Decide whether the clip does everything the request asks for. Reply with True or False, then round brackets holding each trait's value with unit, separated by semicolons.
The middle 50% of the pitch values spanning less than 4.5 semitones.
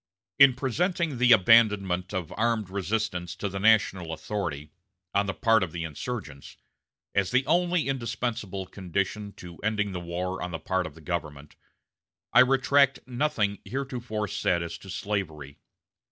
False (5.2 semitones)